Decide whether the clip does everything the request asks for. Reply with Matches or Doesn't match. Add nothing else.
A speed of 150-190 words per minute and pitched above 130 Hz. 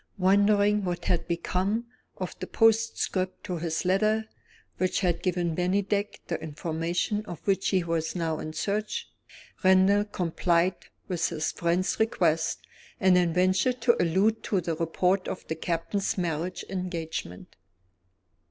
Doesn't match